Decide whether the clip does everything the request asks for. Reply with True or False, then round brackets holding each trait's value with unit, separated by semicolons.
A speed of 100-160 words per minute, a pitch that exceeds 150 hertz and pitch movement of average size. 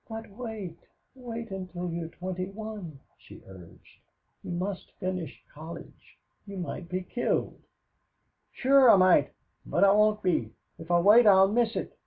True (150 wpm; 190 Hz; 3.8 semitones)